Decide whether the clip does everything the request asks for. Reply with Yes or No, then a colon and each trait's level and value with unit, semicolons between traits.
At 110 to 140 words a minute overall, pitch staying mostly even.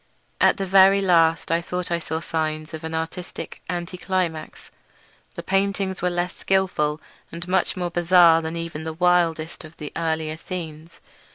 No: average, 165 wpm; narrow, 2.1 semitones